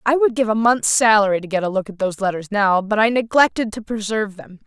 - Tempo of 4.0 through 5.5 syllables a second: No, 6.2 syllables/s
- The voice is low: No, high, 210 Hz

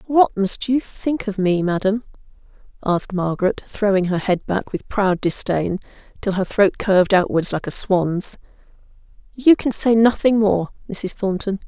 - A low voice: No, high, 200 Hz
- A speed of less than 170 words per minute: Yes, average, 160 wpm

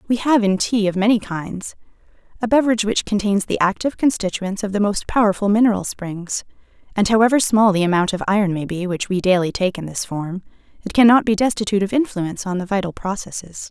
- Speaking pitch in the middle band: No, high, 200 Hz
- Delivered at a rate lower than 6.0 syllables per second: No, 6.1 syllables/s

